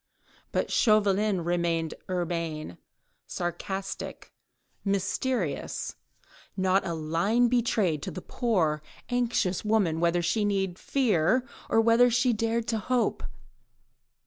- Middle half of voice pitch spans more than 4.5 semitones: Yes, average, 5.0 semitones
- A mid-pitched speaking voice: No, high, 195 Hz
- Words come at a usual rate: No, slow, 105 wpm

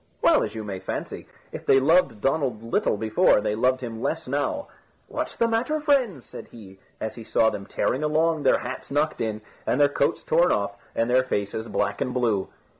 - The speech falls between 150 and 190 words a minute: No, average, 200 wpm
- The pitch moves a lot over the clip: Yes, wide, 5.9 semitones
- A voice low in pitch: Yes, low, 125 Hz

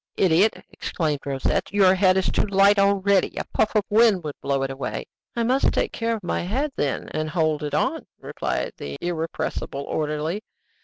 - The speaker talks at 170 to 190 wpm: Yes, average, 185 wpm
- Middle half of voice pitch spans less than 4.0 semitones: No, average, 5.1 semitones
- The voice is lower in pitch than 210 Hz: Yes, medium, 185 Hz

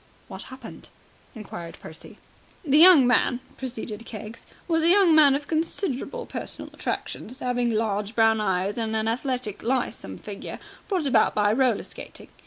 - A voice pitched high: Yes, high, 245 Hz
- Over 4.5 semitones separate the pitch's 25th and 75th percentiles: Yes, average, 4.9 semitones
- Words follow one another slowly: No, average, 150 wpm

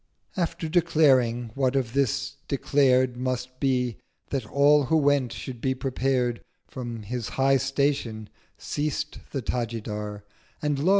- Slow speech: Yes, slow, 130 wpm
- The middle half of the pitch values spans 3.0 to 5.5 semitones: No, narrow, 2.6 semitones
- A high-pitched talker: No, low, 130 Hz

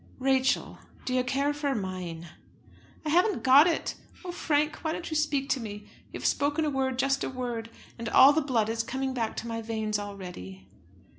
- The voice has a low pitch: No, very high, 260 Hz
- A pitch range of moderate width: Yes, average, 4.6 semitones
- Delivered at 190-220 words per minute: Yes, average, 200 wpm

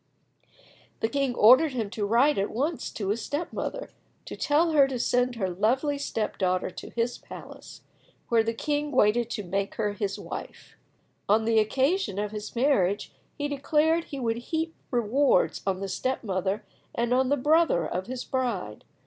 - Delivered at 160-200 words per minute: Yes, average, 175 wpm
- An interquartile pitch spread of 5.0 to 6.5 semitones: Yes, wide, 5.6 semitones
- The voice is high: Yes, high, 240 Hz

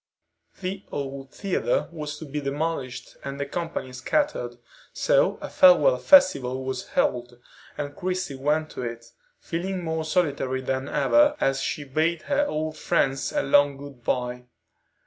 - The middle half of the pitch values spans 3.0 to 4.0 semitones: No, average, 5.1 semitones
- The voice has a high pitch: No, medium, 145 Hz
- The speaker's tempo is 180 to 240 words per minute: No, average, 145 wpm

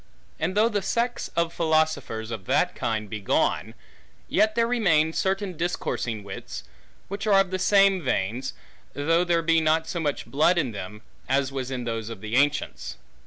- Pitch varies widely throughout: Yes, wide, 7.7 semitones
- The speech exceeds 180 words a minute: No, average, 175 wpm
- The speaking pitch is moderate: Yes, medium, 160 Hz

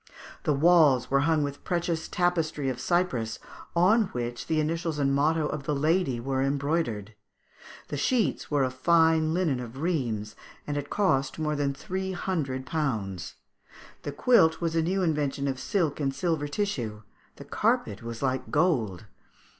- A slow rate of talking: No, average, 160 wpm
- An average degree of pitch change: Yes, average, 4.2 semitones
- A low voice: No, medium, 145 Hz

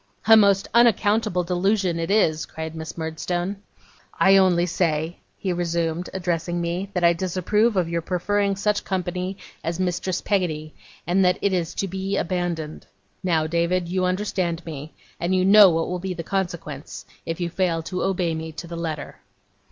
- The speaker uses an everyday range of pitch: No, narrow, 2.3 semitones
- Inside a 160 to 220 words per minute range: Yes, average, 170 wpm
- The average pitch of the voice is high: No, medium, 175 Hz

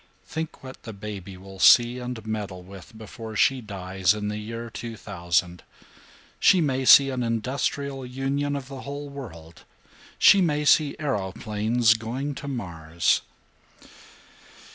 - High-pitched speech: No, low, 115 Hz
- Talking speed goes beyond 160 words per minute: No, slow, 135 wpm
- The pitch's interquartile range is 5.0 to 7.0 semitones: Yes, wide, 5.5 semitones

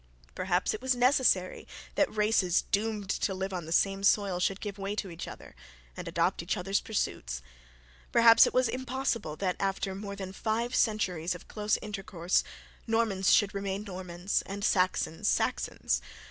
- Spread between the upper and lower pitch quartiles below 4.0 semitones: Yes, average, 2.9 semitones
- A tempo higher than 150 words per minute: Yes, average, 160 wpm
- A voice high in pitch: Yes, high, 195 Hz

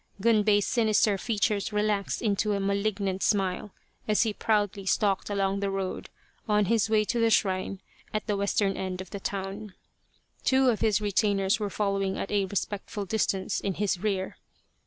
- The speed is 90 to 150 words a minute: No, average, 165 wpm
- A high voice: Yes, high, 200 Hz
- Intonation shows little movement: Yes, narrow, 1.5 semitones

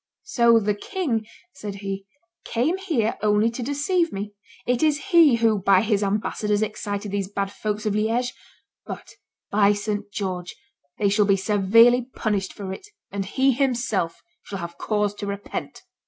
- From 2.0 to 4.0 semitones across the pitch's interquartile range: Yes, average, 3.1 semitones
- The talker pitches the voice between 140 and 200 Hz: No, high, 210 Hz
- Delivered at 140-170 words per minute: Yes, average, 160 wpm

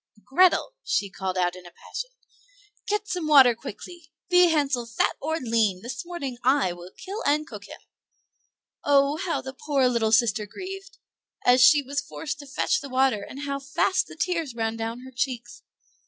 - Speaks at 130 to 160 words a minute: No, average, 180 wpm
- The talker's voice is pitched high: Yes, very high, 275 Hz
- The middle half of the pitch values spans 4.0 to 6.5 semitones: Yes, wide, 5.4 semitones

